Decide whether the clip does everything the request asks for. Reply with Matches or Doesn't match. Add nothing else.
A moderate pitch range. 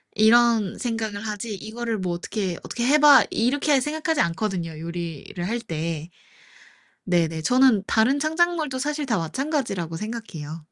Doesn't match